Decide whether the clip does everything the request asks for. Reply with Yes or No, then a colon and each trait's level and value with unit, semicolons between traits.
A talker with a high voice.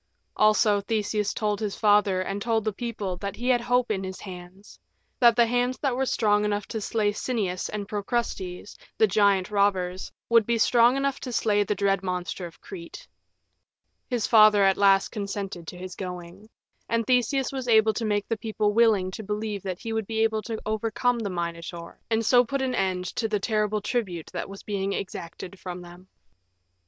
Yes: high, 210 Hz